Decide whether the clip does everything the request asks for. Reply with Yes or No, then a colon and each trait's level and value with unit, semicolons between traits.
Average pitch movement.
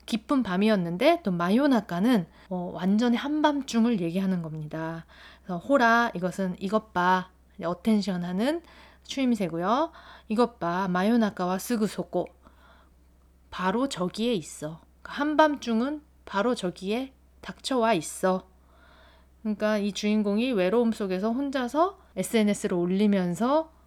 Yes: average, 5.0 semitones